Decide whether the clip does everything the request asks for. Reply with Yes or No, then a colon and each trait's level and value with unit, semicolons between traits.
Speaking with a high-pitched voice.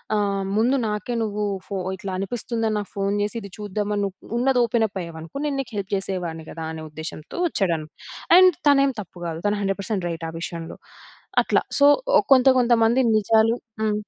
Yes: high, 205 Hz